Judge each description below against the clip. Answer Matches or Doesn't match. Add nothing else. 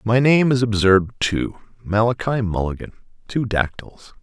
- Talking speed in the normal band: Doesn't match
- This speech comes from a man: Matches